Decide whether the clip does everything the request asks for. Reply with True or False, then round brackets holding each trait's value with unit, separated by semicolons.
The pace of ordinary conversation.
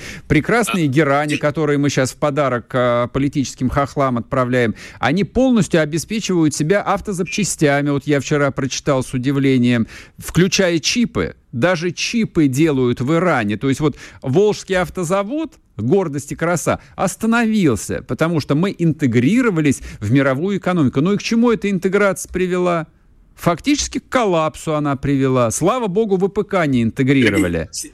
True (130 wpm)